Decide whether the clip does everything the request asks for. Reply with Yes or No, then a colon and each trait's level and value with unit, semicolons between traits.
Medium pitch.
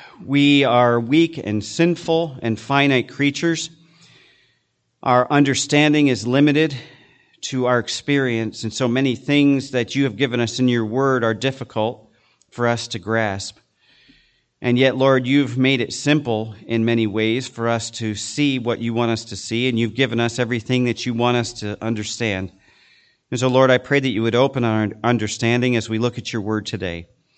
No: low, 125 Hz